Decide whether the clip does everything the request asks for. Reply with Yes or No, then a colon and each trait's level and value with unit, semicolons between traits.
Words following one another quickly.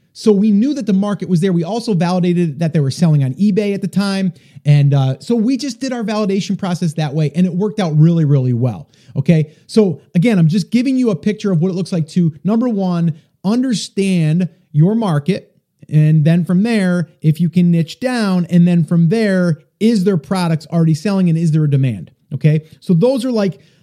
Yes: fast, 215 wpm